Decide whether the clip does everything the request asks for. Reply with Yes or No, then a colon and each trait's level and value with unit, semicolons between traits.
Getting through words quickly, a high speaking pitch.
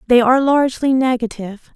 No: slow, 135 wpm; very high, 250 Hz